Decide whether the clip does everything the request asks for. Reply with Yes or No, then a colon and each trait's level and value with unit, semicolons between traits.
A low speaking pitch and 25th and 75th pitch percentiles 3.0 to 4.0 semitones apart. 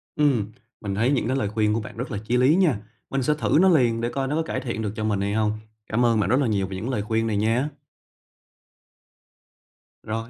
Yes: low, 115 Hz; average, 3.6 semitones